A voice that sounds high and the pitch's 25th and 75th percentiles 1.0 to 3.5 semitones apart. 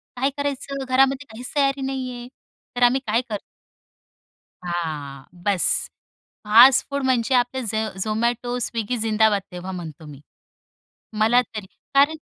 No: high, 235 Hz; average, 4.0 semitones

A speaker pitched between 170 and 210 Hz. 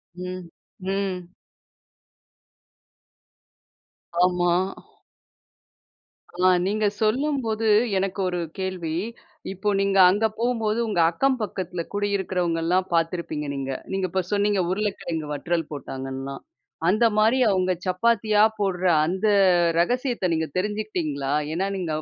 Yes: medium, 185 Hz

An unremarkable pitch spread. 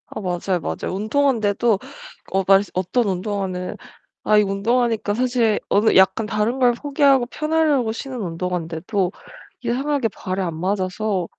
Yes: average, 4.6 semitones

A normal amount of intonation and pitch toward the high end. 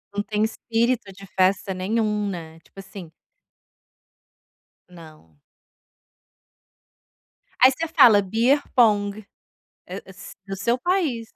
Yes: average, 3.8 semitones; high, 210 Hz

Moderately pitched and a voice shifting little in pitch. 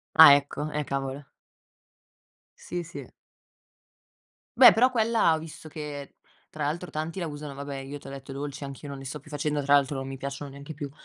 Yes: medium, 145 Hz; narrow, 2.0 semitones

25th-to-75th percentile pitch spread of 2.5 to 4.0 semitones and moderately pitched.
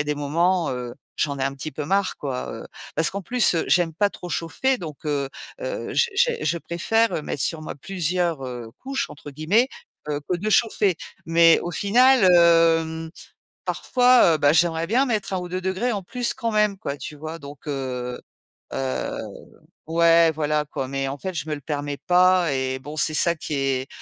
No: average, 4.7 semitones; medium, 165 Hz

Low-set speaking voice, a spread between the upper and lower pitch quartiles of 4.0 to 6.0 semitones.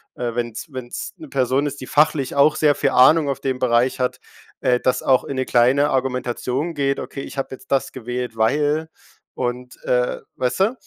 No: low, 130 Hz; narrow, 2.4 semitones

